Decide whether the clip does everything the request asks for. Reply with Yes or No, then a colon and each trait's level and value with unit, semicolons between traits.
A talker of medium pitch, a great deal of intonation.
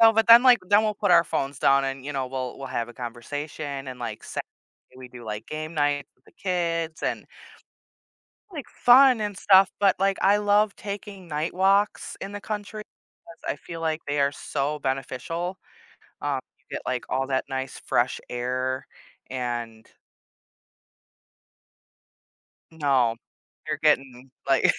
Yes: medium, 150 Hz; wide, 6.9 semitones